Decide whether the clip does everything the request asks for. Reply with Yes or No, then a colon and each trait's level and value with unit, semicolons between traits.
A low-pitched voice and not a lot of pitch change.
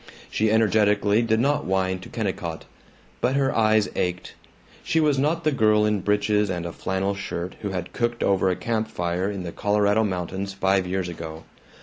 No: low, 100 Hz; average, 3.0 semitones